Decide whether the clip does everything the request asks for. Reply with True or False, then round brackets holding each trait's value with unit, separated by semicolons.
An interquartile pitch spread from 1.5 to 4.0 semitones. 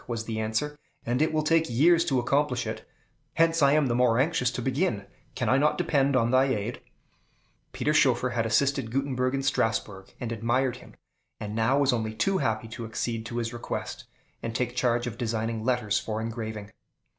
True (3.5 semitones)